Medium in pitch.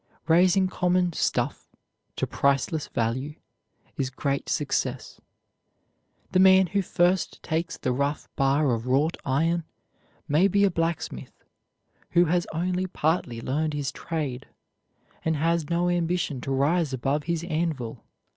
Yes: medium, 160 Hz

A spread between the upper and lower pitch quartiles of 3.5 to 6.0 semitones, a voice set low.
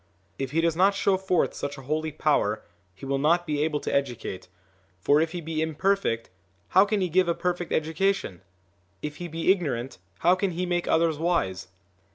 No: average, 4.0 semitones; medium, 160 Hz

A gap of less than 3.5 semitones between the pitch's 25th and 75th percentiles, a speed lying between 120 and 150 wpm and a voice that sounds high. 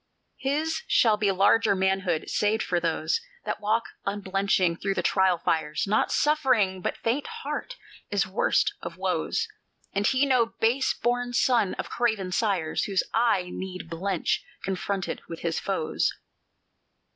No: average, 4.3 semitones; average, 145 wpm; high, 200 Hz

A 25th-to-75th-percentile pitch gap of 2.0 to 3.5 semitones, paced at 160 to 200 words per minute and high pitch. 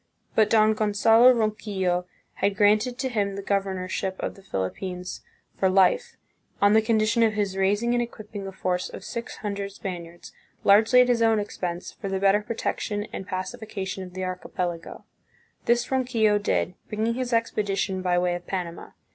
Yes: average, 2.9 semitones; average, 165 wpm; high, 205 Hz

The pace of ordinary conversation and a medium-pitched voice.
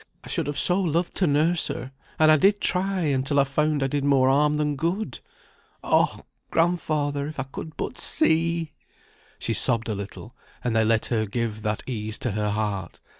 Yes: average, 190 wpm; medium, 145 Hz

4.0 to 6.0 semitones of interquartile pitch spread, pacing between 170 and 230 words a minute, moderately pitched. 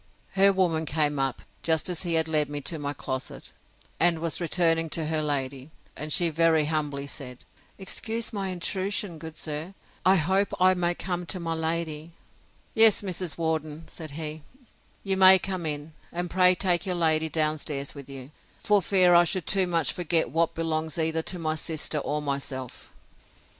No: average, 2.8 semitones; average, 175 wpm; medium, 160 Hz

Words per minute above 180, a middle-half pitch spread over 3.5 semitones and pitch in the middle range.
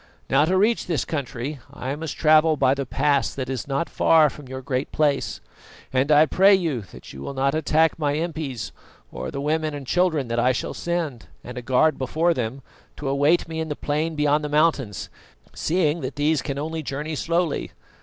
No: average, 200 wpm; average, 2.9 semitones; medium, 150 Hz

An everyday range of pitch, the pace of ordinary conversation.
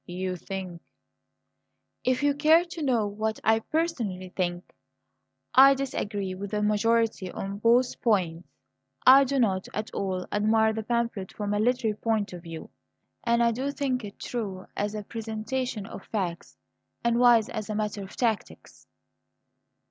Yes: average, 3.6 semitones; average, 155 wpm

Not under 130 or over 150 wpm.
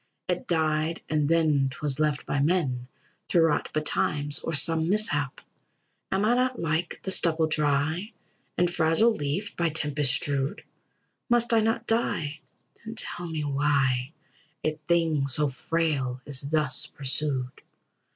Yes: average, 140 wpm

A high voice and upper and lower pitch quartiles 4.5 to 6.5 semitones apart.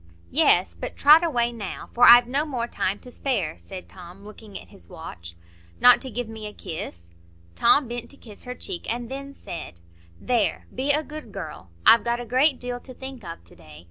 Yes: high, 240 Hz; average, 5.2 semitones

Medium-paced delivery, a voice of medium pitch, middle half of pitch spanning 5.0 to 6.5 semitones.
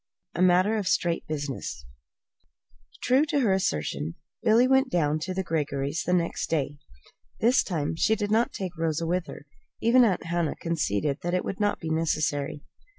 Yes: average, 170 wpm; medium, 170 Hz; average, 5.3 semitones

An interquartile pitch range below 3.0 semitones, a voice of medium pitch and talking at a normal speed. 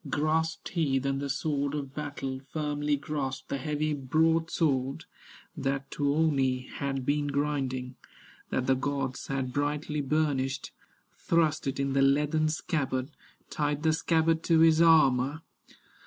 No: narrow, 2.4 semitones; medium, 145 Hz; slow, 130 wpm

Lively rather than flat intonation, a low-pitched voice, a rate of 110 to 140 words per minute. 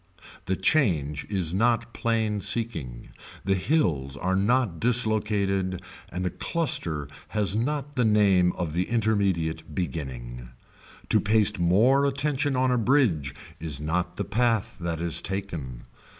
Yes: wide, 6.2 semitones; very low, 95 Hz; slow, 135 wpm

